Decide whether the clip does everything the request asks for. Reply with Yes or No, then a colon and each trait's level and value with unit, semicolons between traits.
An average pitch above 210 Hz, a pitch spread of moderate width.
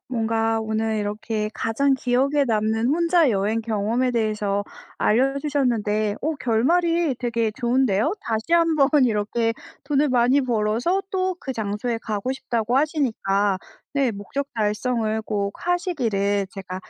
Yes: high, 230 Hz; average, 4.5 semitones